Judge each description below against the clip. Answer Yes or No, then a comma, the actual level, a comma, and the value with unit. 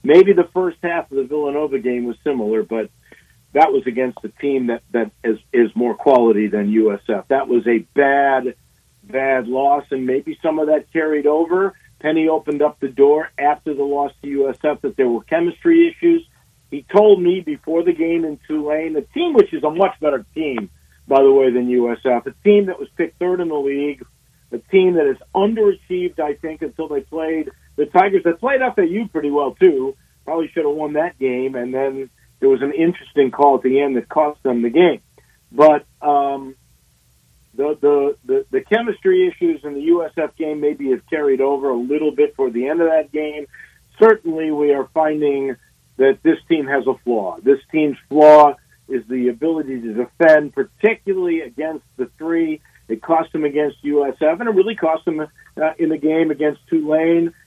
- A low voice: No, medium, 150 Hz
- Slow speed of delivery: No, average, 195 wpm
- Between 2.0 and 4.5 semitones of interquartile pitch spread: Yes, average, 3.8 semitones